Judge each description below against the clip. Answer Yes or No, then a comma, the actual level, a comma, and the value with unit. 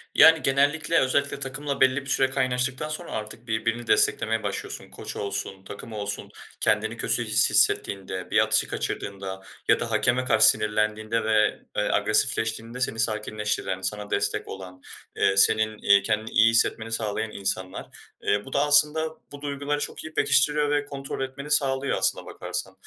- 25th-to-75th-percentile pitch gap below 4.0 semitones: No, average, 4.6 semitones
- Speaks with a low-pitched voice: Yes, low, 115 Hz